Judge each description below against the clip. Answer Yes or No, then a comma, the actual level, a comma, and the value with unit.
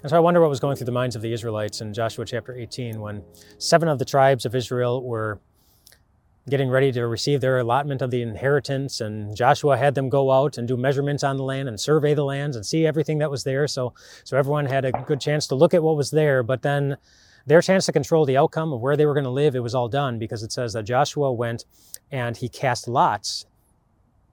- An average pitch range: Yes, average, 3.4 semitones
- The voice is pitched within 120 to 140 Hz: Yes, low, 135 Hz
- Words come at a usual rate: No, fast, 240 wpm